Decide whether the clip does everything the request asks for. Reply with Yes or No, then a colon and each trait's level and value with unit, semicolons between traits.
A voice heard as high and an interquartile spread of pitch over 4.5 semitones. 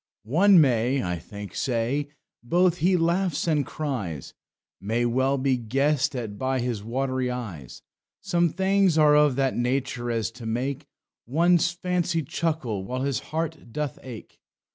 No: low, 135 Hz; average, 5.1 semitones